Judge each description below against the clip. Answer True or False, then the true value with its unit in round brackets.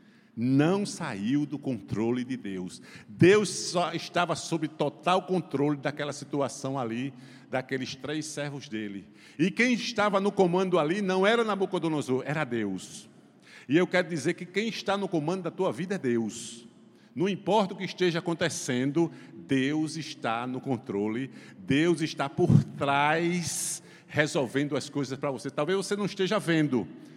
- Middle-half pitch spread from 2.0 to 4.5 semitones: False (5.1 semitones)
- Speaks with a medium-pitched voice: True (155 Hz)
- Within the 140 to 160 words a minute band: True (150 wpm)